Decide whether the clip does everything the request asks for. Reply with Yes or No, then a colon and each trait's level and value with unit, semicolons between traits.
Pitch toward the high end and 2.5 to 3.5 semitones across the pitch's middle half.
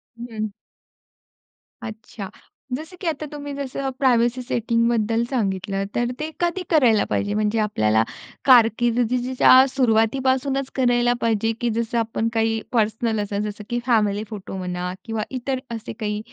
Yes: high, 230 Hz; average, 3.0 semitones